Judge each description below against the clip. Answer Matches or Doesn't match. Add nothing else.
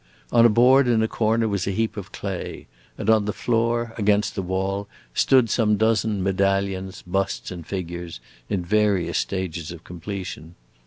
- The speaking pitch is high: Doesn't match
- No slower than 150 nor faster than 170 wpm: Matches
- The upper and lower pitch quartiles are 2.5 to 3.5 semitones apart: Matches